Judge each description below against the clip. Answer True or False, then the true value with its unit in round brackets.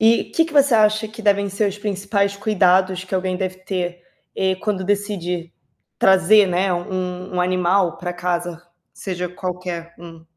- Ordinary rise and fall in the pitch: False (2.2 semitones)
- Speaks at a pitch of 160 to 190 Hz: True (185 Hz)